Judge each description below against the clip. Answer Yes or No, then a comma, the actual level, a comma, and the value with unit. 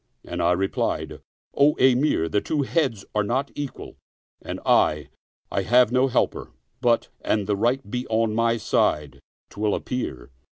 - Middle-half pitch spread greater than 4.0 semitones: Yes, average, 4.4 semitones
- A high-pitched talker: No, low, 115 Hz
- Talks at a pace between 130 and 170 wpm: Yes, average, 155 wpm